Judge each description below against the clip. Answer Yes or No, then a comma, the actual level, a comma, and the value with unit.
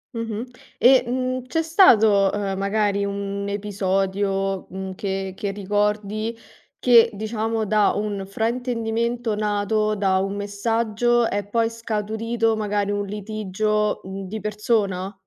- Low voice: No, high, 210 Hz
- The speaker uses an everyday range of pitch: No, narrow, 2.1 semitones